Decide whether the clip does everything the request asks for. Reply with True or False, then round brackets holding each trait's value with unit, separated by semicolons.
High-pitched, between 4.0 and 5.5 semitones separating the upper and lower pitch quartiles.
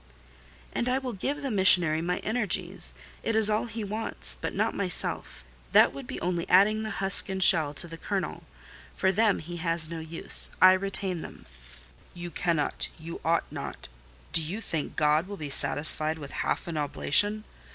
False (180 Hz; 4.3 semitones)